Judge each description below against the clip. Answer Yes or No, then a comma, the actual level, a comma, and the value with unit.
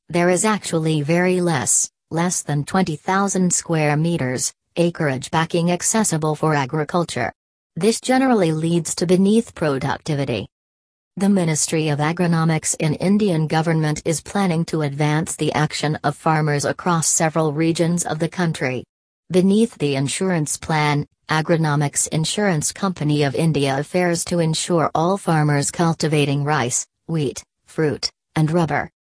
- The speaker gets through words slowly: Yes, slow, 130 wpm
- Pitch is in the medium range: Yes, medium, 160 Hz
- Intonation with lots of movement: No, average, 3.0 semitones